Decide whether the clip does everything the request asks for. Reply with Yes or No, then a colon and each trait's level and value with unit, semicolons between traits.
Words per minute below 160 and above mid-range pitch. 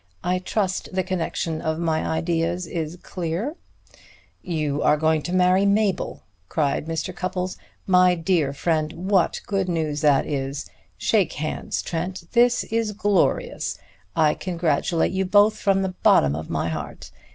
No: average, 140 wpm; medium, 175 Hz